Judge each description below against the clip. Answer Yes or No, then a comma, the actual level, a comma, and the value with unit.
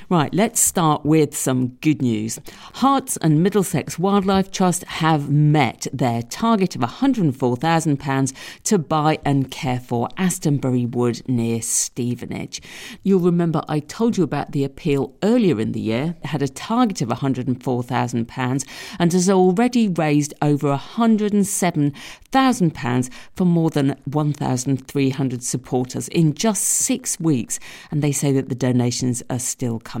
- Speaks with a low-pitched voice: No, medium, 150 Hz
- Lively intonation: Yes, wide, 6.1 semitones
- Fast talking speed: No, average, 140 wpm